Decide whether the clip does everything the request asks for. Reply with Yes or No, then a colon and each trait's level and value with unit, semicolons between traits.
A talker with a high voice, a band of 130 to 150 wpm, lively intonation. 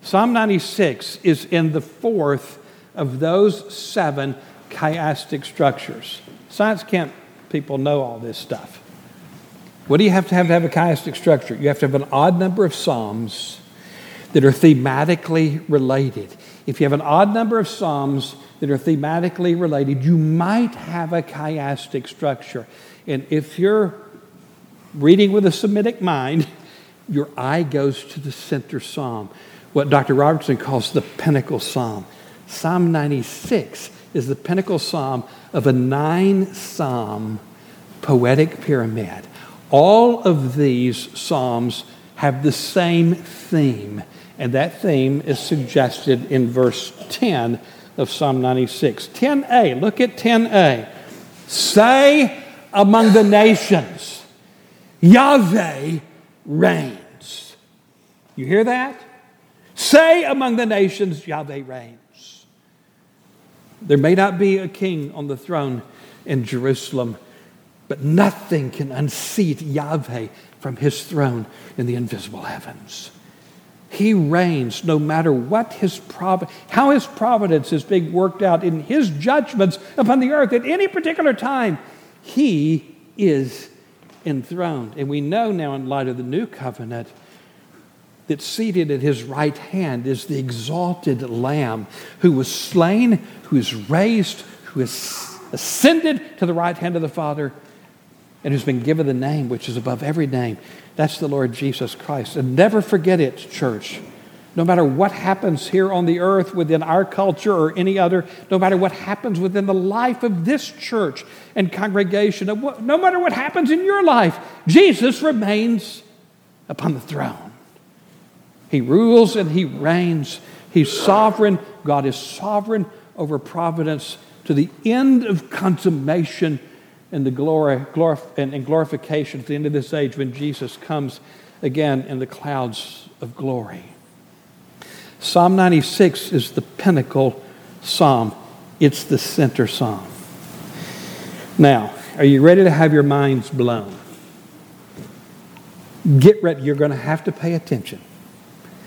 No: medium, 160 Hz; average, 140 wpm; wide, 6.1 semitones